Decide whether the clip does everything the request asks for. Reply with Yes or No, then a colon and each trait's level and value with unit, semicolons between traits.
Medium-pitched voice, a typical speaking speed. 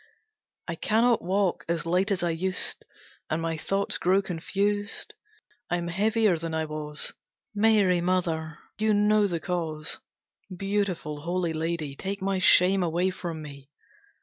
Yes: medium, 180 Hz; average, 145 wpm